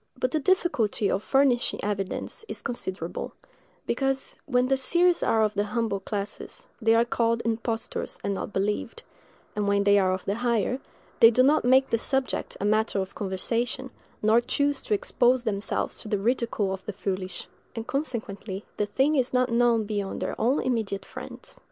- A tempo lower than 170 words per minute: No, average, 175 wpm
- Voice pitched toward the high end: Yes, high, 225 Hz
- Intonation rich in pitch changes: No, average, 3.9 semitones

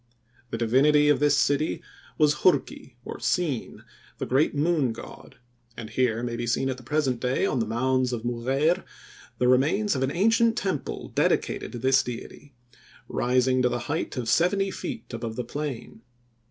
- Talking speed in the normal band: Yes, average, 170 wpm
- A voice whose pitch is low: Yes, low, 130 Hz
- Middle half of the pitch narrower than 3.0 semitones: No, average, 3.7 semitones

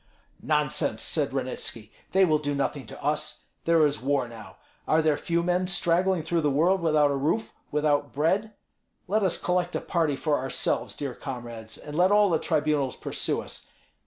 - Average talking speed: Yes, average, 180 wpm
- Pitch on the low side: No, medium, 155 Hz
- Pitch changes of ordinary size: Yes, average, 3.6 semitones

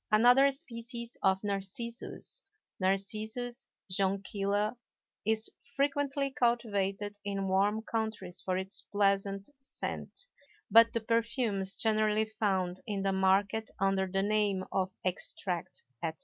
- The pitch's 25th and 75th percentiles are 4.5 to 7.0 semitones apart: No, average, 2.9 semitones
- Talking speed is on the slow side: Yes, slow, 110 wpm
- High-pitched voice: Yes, high, 205 Hz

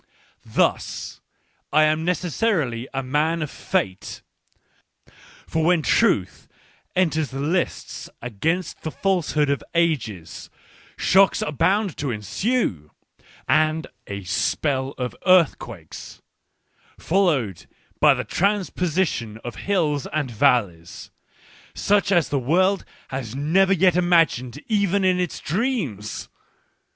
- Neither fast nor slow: No, slow, 110 wpm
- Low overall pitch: No, medium, 155 Hz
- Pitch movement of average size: No, wide, 6.6 semitones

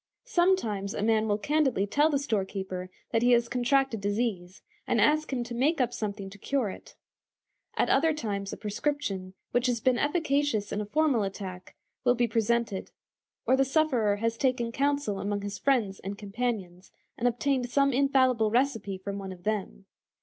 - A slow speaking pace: No, average, 175 wpm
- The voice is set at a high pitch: Yes, high, 230 Hz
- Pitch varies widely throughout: No, average, 5.0 semitones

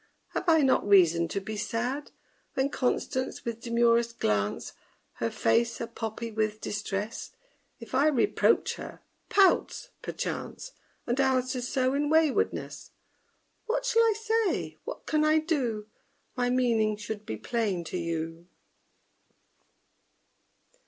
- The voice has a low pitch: No, high, 235 Hz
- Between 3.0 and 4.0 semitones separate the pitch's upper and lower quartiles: No, average, 5.2 semitones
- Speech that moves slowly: Yes, slow, 125 wpm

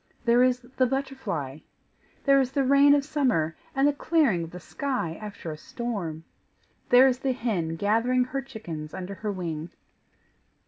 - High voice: Yes, high, 240 Hz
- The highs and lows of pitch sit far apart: Yes, wide, 7.6 semitones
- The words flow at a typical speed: Yes, average, 165 wpm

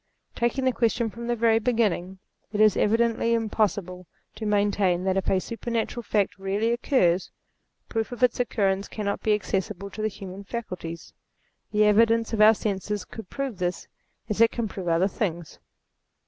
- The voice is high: Yes, high, 210 Hz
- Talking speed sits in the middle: Yes, average, 170 wpm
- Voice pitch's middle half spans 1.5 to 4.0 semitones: Yes, average, 3.1 semitones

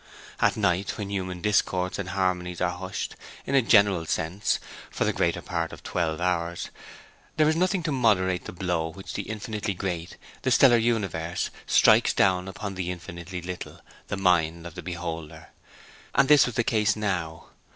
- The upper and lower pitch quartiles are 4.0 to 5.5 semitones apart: No, average, 3.3 semitones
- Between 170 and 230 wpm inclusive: Yes, average, 175 wpm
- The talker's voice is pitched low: Yes, very low, 95 Hz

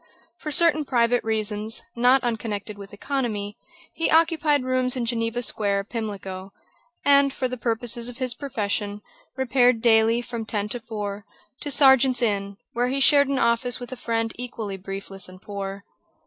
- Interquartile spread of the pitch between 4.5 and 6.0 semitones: No, average, 3.7 semitones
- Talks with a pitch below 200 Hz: No, high, 235 Hz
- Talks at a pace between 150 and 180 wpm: Yes, average, 160 wpm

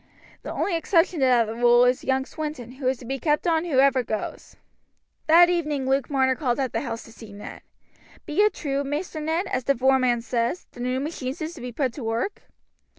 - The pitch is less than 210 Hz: No, very high, 265 Hz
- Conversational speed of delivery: No, fast, 210 wpm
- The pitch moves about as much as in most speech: Yes, average, 4.0 semitones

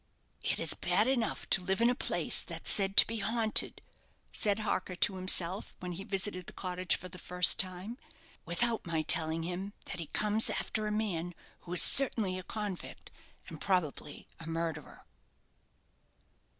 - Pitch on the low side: No, medium, 185 Hz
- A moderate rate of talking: Yes, average, 165 wpm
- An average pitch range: Yes, average, 3.3 semitones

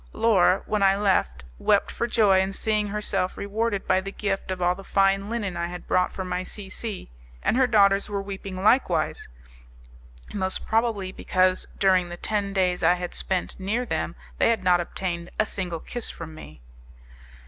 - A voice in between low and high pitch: No, high, 195 Hz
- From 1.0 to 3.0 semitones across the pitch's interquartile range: Yes, narrow, 2.4 semitones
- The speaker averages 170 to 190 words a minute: Yes, average, 180 wpm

